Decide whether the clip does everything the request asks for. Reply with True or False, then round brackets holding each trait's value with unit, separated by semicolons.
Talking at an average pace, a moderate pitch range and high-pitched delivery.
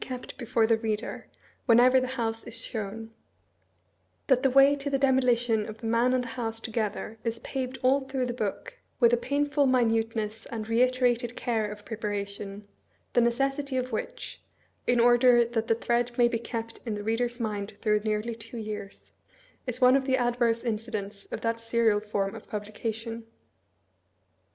False (175 wpm; 2.3 semitones; 230 Hz)